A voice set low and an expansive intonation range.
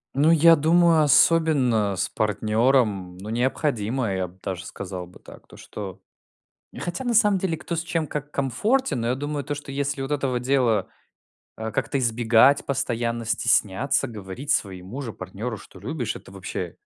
Yes: low, 125 Hz; wide, 5.7 semitones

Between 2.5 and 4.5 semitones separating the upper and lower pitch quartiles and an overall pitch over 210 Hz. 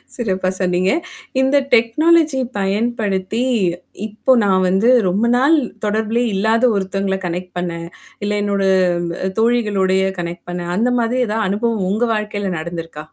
No: average, 3.6 semitones; high, 205 Hz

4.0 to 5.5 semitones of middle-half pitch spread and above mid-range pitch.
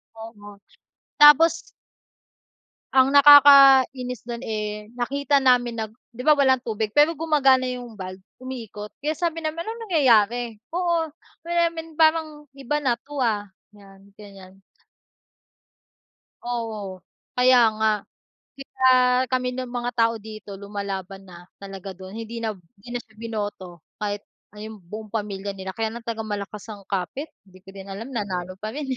Yes: average, 4.5 semitones; high, 225 Hz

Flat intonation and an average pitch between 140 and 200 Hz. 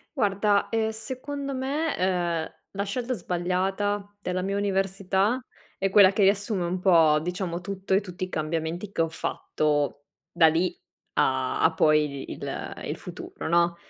No: average, 3.2 semitones; medium, 185 Hz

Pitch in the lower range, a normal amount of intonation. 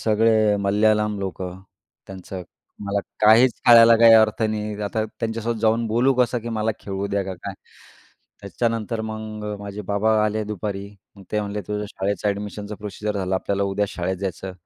No: low, 105 Hz; narrow, 1.8 semitones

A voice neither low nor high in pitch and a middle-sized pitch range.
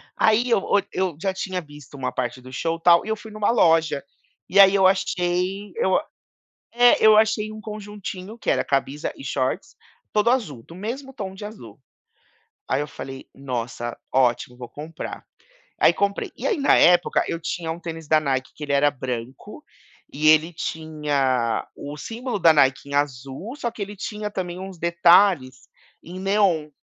No: medium, 170 Hz; wide, 6.4 semitones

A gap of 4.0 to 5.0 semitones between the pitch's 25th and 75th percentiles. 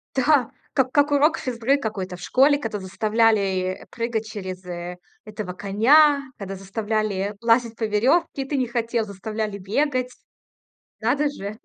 Yes: average, 4.5 semitones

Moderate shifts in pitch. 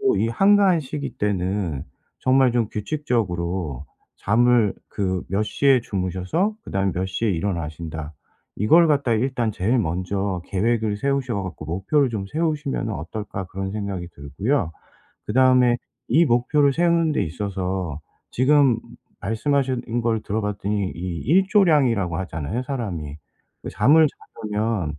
No: wide, 6.0 semitones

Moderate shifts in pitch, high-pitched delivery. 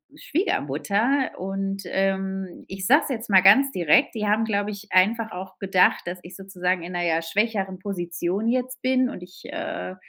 Yes: average, 3.5 semitones; high, 195 Hz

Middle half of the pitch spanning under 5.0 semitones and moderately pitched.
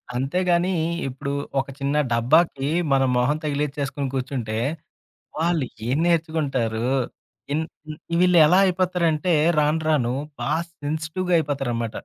Yes: average, 3.7 semitones; medium, 150 Hz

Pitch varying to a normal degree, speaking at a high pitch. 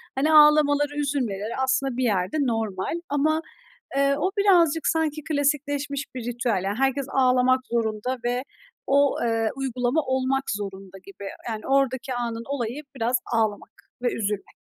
Yes: average, 4.0 semitones; very high, 260 Hz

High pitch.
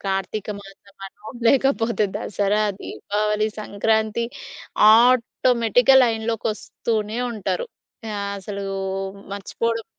Yes: high, 215 Hz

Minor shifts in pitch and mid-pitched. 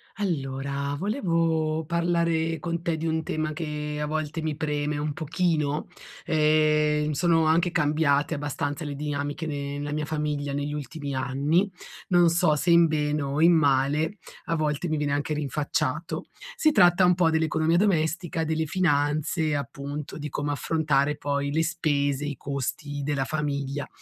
Yes: narrow, 2.0 semitones; medium, 150 Hz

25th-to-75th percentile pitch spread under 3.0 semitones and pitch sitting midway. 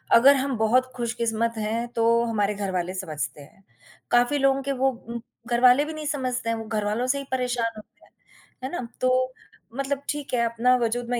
No: narrow, 2.4 semitones; high, 240 Hz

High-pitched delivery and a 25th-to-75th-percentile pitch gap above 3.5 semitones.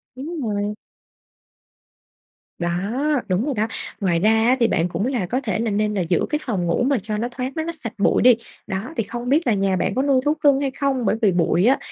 Yes: high, 225 Hz; average, 5.2 semitones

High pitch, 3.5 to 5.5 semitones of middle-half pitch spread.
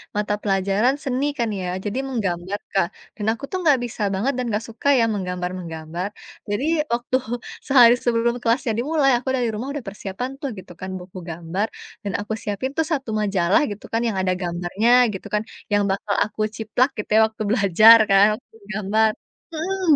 Yes: high, 210 Hz; average, 4.1 semitones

